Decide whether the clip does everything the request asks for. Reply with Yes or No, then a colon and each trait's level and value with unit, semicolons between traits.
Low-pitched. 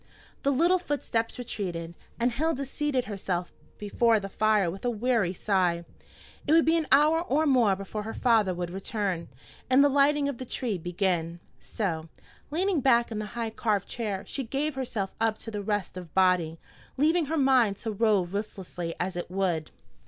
No: high, 220 Hz